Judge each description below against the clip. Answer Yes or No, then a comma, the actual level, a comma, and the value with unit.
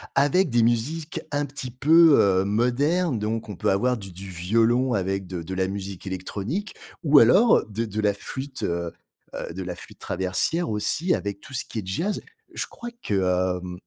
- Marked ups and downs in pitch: Yes, wide, 6.8 semitones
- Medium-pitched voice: No, low, 110 Hz